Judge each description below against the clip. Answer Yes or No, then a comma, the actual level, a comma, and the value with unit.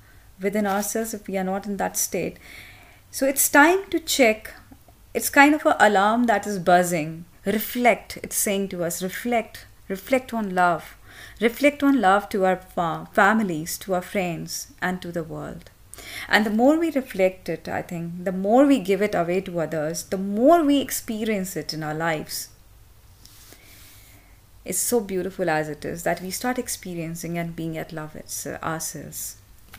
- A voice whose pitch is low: No, medium, 185 Hz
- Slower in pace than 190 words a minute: Yes, average, 175 wpm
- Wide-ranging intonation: Yes, wide, 6.1 semitones